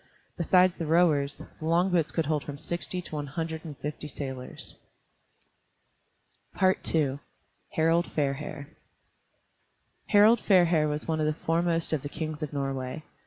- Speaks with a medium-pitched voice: Yes, medium, 155 Hz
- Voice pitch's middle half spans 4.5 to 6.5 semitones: No, average, 2.7 semitones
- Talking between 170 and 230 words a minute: No, average, 140 wpm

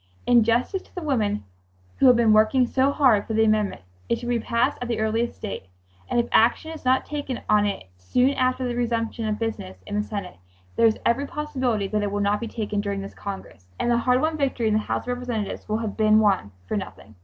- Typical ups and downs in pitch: Yes, average, 3.1 semitones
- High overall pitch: Yes, high, 225 Hz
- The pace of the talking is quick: Yes, fast, 235 wpm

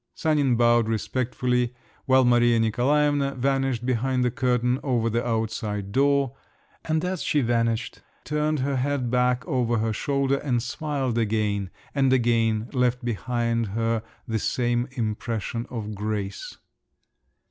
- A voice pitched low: Yes, low, 120 Hz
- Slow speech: Yes, slow, 130 wpm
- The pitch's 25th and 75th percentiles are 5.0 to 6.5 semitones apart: No, average, 2.7 semitones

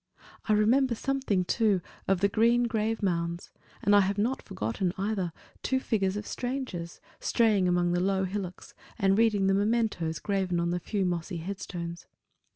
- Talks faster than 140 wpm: Yes, average, 165 wpm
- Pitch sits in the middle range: No, high, 195 Hz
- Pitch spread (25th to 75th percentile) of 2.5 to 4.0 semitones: Yes, average, 3.7 semitones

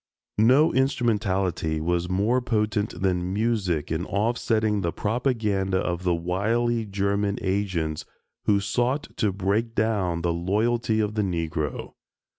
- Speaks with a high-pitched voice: No, low, 100 Hz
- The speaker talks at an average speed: No, slow, 130 wpm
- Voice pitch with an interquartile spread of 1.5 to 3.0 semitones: No, average, 3.9 semitones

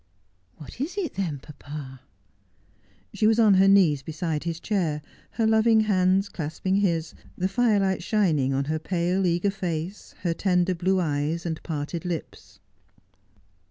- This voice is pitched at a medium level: Yes, medium, 175 Hz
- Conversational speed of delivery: Yes, average, 155 wpm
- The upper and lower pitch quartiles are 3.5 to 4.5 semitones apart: Yes, average, 4.2 semitones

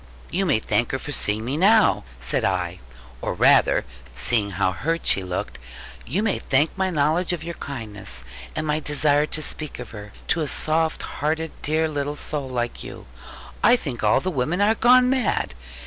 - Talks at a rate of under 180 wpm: No, average, 185 wpm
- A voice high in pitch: No, medium, 150 Hz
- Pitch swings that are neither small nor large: No, wide, 6.3 semitones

